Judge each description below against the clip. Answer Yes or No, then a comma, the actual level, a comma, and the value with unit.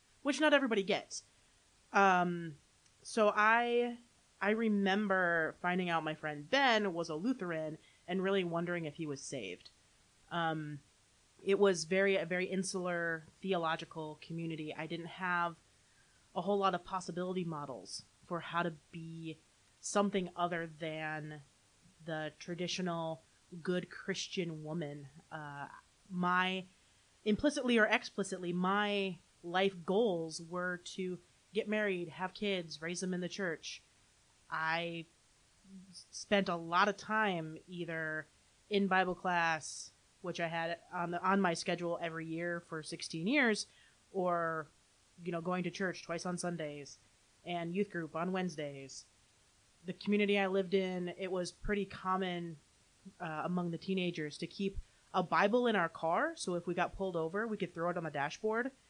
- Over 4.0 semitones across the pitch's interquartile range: No, average, 3.0 semitones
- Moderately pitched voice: Yes, medium, 175 Hz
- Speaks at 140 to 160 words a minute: Yes, average, 145 wpm